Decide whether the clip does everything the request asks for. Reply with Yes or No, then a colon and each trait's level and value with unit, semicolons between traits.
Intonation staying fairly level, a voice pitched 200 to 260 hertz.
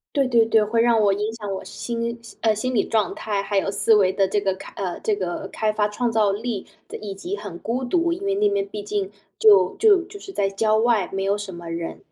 No: average, 3.2 semitones; high, 215 Hz